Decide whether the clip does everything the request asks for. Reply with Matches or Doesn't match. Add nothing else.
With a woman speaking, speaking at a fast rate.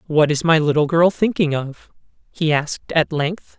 Doesn't match